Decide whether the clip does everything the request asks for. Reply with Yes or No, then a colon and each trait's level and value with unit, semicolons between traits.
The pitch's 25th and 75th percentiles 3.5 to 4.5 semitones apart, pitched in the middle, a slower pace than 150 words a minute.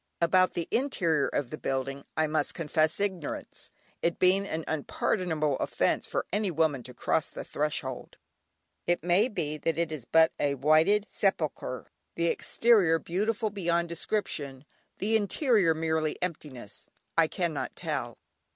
Yes: average, 4.0 semitones; medium, 165 Hz; average, 140 wpm